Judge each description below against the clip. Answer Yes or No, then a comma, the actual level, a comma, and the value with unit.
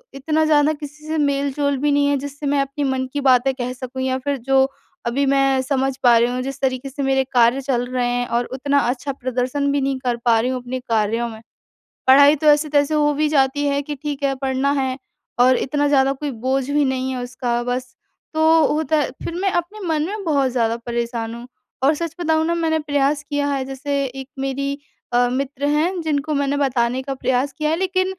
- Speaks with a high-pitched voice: Yes, very high, 275 Hz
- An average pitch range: No, narrow, 2.3 semitones